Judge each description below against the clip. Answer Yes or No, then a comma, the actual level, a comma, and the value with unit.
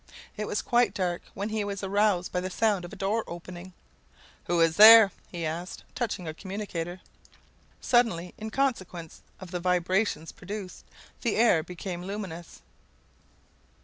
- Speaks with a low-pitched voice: No, medium, 185 Hz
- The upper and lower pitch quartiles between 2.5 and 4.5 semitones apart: Yes, average, 3.3 semitones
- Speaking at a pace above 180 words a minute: No, average, 145 wpm